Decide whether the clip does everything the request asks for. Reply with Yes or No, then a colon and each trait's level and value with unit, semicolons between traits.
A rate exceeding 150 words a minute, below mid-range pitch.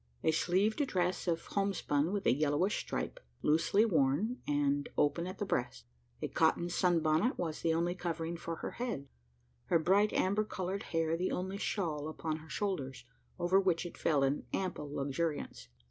No: average, 170 wpm; medium, 170 Hz